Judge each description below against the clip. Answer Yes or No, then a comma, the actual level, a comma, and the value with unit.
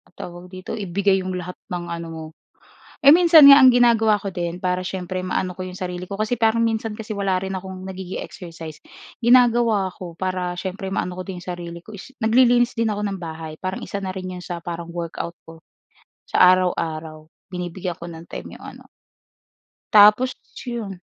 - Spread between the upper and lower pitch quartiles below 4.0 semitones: Yes, average, 3.5 semitones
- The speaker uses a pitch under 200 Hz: Yes, medium, 185 Hz